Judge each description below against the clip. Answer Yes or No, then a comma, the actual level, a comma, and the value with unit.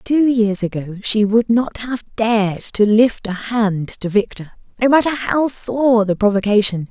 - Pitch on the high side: Yes, high, 220 Hz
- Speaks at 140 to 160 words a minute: No, average, 175 wpm